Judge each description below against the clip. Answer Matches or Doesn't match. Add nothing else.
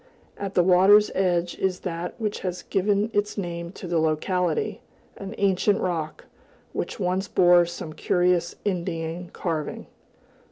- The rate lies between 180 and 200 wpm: Doesn't match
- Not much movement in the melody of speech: Matches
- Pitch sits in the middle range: Matches